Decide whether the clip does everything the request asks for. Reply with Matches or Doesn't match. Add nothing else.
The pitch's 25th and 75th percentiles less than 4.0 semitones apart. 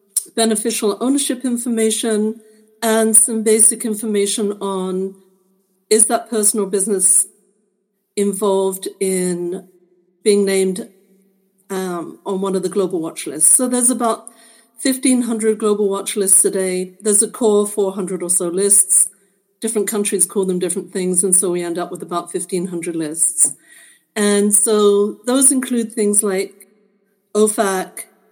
Matches